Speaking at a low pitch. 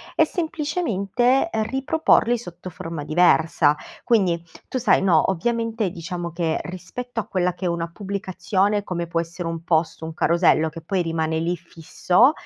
No: medium, 180 Hz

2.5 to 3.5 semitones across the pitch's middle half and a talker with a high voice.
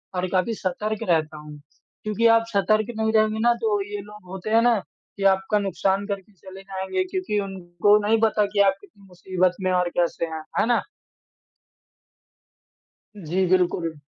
Yes: average, 2.8 semitones; high, 195 Hz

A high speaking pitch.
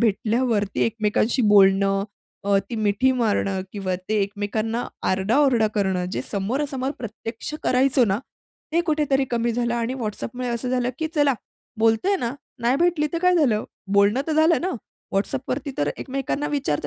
Yes: high, 235 Hz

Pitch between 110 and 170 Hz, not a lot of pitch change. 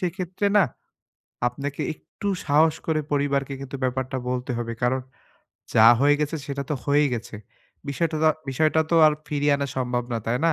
No: medium, 140 Hz; average, 3.2 semitones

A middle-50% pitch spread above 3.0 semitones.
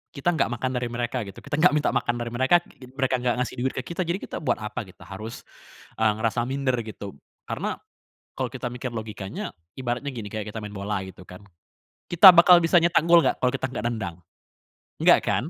Yes: average, 4.3 semitones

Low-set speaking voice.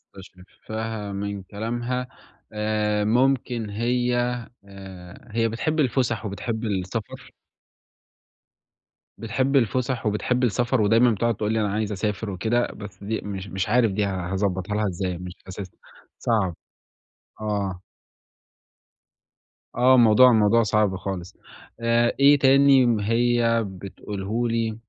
Yes: low, 110 Hz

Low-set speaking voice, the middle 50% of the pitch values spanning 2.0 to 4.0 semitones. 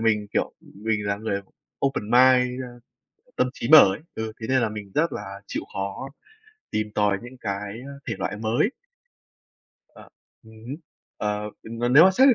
Yes: low, 110 Hz; average, 3.7 semitones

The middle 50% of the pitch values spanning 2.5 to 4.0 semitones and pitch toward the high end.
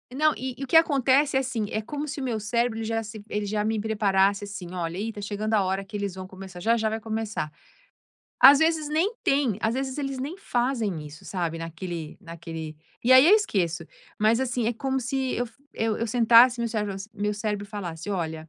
No: average, 4.9 semitones; high, 220 Hz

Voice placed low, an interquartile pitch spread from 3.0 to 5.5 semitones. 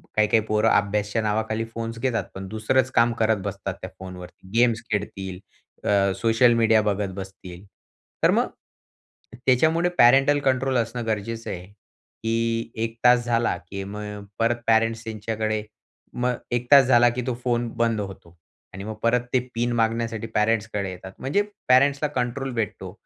No: low, 115 Hz; narrow, 2.6 semitones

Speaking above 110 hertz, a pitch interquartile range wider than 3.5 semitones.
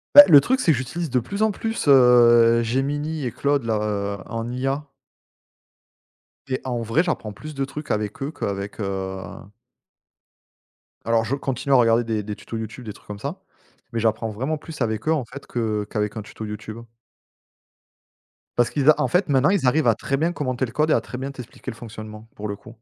Yes: low, 120 Hz; average, 4.6 semitones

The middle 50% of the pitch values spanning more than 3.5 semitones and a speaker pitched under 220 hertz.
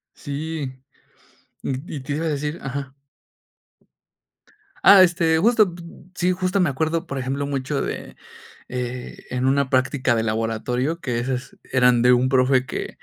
Yes: average, 4.1 semitones; low, 135 Hz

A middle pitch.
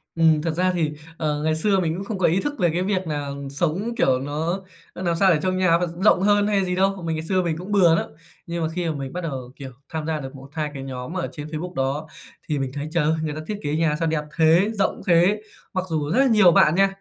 Yes: medium, 165 Hz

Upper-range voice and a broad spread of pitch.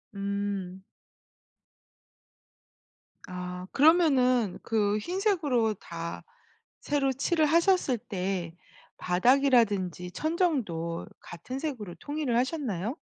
Yes: high, 230 Hz; wide, 7.8 semitones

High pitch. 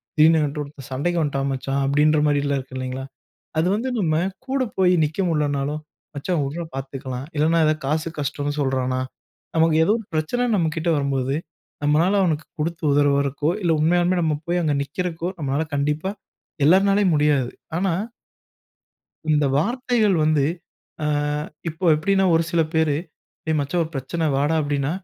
No: medium, 155 Hz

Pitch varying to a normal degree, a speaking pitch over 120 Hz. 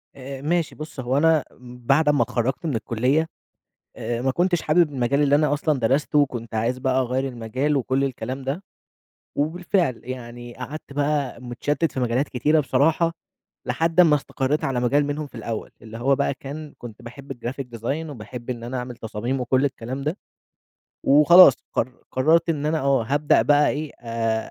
Yes: average, 3.4 semitones; low, 135 Hz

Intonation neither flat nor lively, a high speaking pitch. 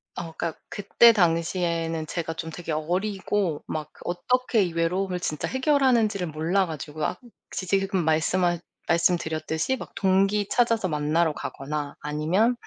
No: average, 3.7 semitones; medium, 175 Hz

